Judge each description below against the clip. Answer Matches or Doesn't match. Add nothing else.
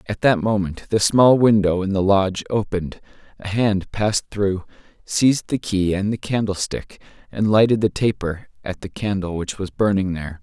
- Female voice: Doesn't match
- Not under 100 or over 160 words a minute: Doesn't match